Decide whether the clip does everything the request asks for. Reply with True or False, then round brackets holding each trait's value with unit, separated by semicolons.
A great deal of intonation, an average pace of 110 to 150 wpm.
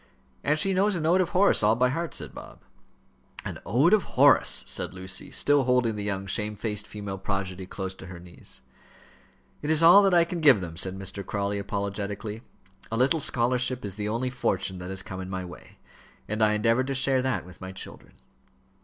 False (5.8 semitones; 200 wpm)